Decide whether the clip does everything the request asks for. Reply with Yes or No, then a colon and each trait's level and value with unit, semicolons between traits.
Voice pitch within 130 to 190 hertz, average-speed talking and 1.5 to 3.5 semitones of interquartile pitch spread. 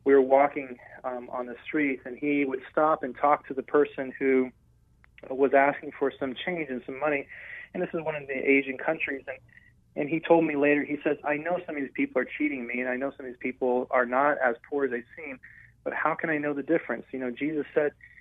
No: medium, 140 Hz; fast, 245 wpm; narrow, 2.6 semitones